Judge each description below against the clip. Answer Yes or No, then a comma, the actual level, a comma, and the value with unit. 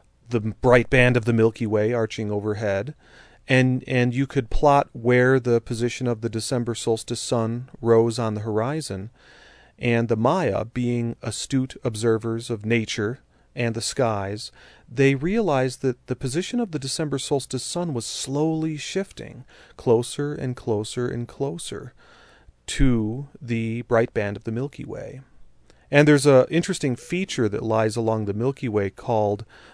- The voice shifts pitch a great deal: No, average, 3.2 semitones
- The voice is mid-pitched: No, low, 120 Hz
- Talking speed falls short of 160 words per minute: Yes, average, 150 wpm